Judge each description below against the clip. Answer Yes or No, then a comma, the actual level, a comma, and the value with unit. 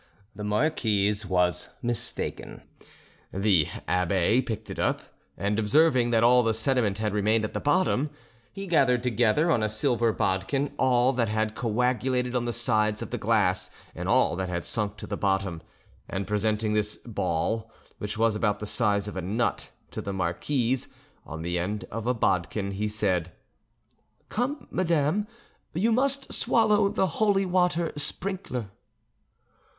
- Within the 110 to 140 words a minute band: No, average, 155 wpm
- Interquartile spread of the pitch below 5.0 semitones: Yes, average, 4.4 semitones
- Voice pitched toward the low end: Yes, low, 110 Hz